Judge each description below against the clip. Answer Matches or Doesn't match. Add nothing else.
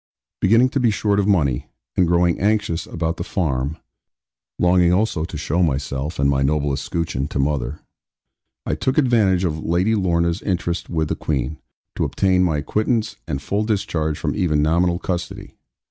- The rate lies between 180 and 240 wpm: Doesn't match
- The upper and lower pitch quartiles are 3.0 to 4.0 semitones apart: Doesn't match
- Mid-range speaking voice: Doesn't match